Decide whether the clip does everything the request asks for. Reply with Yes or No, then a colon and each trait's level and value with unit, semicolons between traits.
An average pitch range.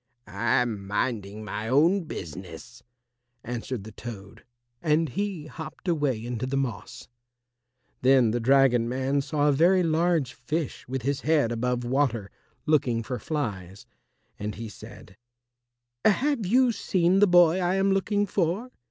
No: wide, 6.6 semitones